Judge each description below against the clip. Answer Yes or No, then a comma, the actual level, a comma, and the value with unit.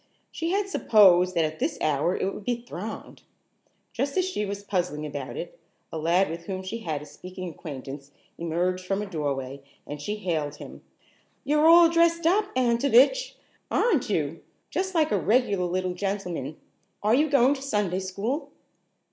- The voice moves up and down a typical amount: No, wide, 8.4 semitones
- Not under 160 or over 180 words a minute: Yes, average, 170 wpm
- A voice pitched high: Yes, high, 195 Hz